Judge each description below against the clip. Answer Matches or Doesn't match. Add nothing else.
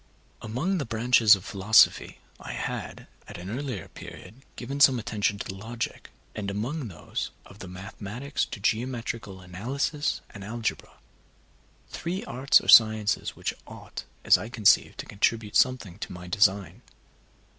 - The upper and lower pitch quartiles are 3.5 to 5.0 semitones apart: Matches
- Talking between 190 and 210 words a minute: Doesn't match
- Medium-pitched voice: Doesn't match